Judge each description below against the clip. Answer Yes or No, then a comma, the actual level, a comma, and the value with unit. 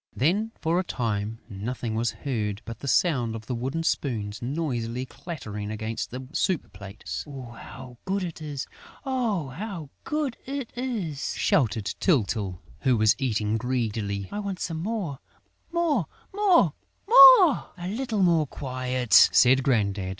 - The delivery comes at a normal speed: Yes, average, 150 wpm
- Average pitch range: No, wide, 8.5 semitones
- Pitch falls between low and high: No, low, 130 Hz